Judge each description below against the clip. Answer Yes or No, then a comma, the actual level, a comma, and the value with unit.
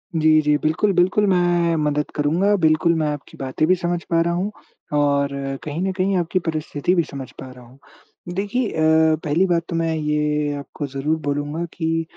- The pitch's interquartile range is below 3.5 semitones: Yes, average, 2.9 semitones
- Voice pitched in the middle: Yes, medium, 160 Hz